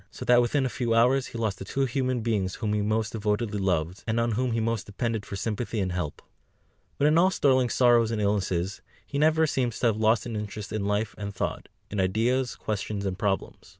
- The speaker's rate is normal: No, fast, 220 wpm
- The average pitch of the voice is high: No, low, 110 Hz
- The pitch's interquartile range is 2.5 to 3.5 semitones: Yes, average, 3.2 semitones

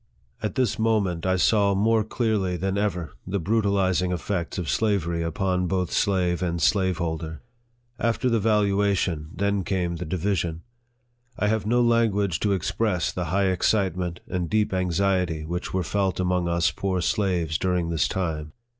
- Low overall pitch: Yes, very low, 95 Hz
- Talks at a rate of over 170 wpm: No, average, 155 wpm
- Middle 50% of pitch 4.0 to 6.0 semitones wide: No, average, 2.9 semitones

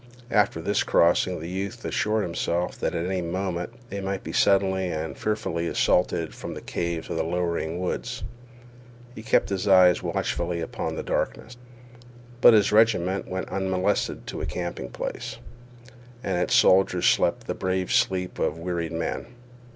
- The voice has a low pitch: Yes, very low, 90 Hz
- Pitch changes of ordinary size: No, narrow, 2.3 semitones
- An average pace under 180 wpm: Yes, average, 160 wpm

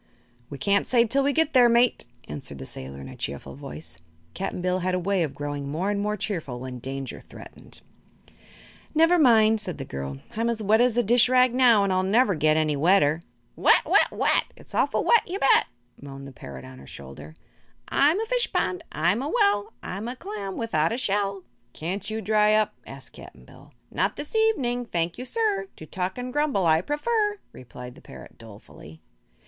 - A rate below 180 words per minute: No, average, 200 wpm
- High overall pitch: Yes, high, 200 Hz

